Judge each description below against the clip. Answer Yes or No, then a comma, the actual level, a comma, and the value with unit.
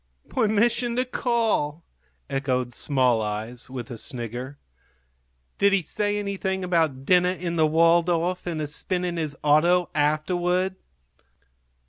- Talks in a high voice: No, medium, 170 Hz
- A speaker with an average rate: No, slow, 125 wpm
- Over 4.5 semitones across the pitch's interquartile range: Yes, average, 4.9 semitones